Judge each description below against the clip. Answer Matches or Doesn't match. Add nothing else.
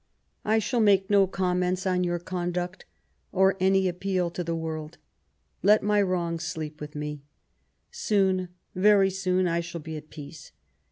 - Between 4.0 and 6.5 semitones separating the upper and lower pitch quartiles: Doesn't match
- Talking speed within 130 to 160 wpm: Doesn't match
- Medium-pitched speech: Matches